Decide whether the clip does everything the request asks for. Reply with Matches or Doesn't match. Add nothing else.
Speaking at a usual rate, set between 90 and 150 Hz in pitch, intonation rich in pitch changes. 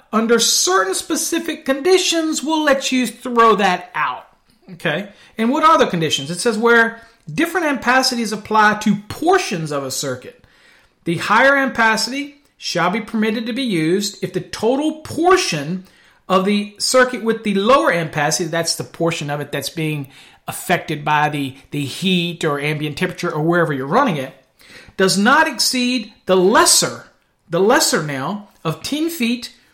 Doesn't match